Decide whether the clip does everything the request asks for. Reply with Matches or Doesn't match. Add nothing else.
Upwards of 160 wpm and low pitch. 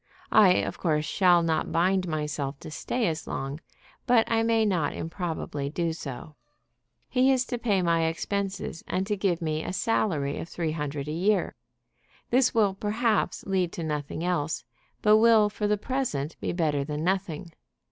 Doesn't match